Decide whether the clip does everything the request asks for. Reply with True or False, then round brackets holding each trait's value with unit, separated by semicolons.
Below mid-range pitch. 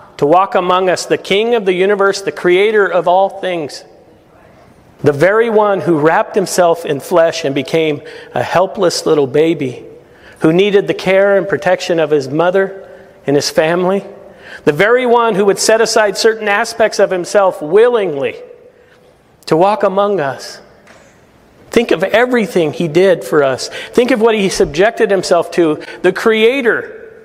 False (195 Hz)